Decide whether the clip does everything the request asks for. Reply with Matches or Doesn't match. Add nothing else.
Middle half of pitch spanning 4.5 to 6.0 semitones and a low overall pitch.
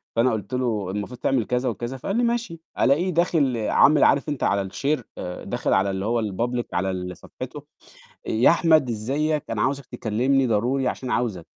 Matches